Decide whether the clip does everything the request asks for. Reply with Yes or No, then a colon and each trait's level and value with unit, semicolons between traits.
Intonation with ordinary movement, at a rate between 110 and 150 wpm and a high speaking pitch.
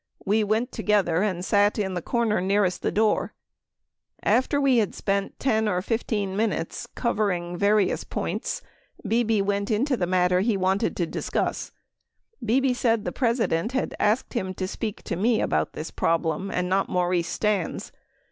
No: average, 3.6 semitones; average, 165 wpm; high, 205 Hz